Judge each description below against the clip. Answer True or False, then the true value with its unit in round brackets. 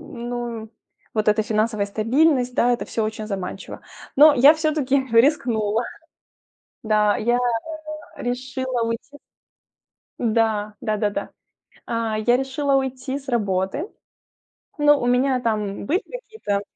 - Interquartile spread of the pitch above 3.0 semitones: True (3.7 semitones)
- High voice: True (240 Hz)